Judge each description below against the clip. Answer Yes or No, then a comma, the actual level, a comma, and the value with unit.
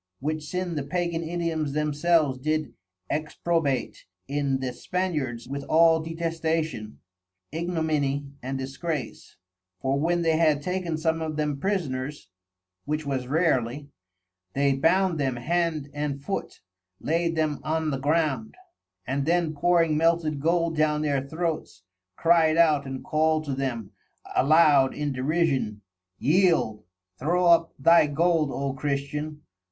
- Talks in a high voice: No, medium, 155 Hz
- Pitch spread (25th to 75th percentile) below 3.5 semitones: Yes, average, 3.0 semitones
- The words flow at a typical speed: No, slow, 130 wpm